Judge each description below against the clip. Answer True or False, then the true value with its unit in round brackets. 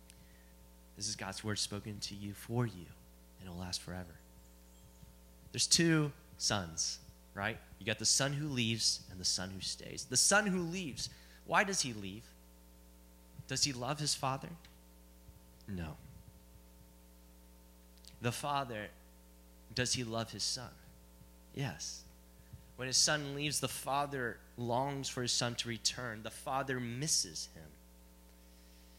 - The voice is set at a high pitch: False (90 Hz)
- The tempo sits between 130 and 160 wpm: True (140 wpm)